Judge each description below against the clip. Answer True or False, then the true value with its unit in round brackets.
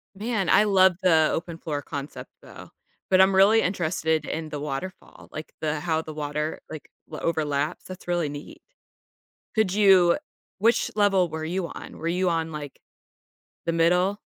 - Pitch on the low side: False (170 Hz)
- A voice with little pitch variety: False (3.4 semitones)